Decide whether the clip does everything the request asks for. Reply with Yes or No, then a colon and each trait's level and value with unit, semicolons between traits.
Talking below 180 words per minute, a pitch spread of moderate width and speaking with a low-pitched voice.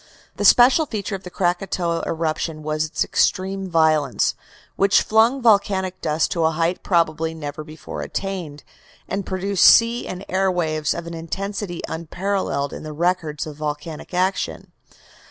No: average, 150 wpm; average, 3.7 semitones; medium, 175 Hz